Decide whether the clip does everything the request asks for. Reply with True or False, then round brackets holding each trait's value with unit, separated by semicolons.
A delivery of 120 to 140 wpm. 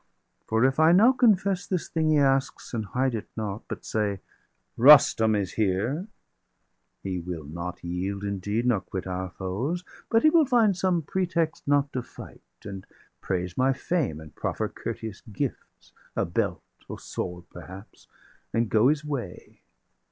False (160 wpm)